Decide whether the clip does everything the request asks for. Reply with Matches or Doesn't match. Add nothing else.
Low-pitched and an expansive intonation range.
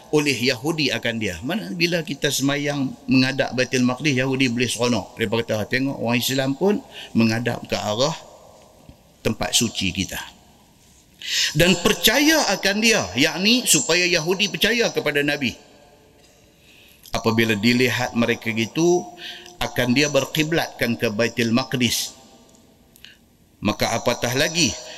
Matches